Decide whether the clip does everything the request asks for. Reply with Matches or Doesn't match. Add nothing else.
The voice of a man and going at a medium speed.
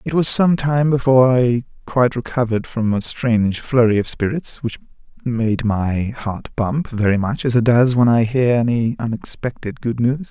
Matches